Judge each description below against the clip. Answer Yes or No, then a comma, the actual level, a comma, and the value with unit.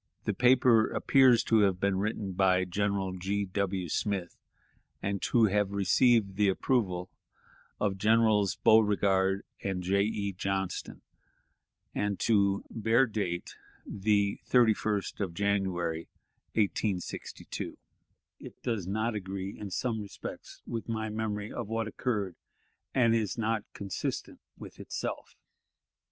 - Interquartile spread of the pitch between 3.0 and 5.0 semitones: No, narrow, 2.4 semitones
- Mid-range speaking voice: No, low, 100 Hz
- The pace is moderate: No, slow, 120 wpm